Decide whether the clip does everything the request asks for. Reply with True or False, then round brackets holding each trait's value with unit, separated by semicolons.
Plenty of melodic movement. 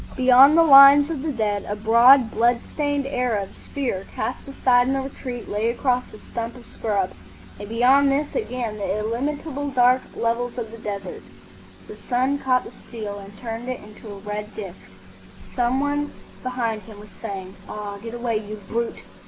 False (3.9 semitones)